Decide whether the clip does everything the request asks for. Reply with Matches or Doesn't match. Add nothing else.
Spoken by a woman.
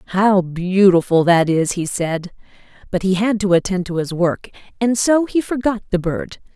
Matches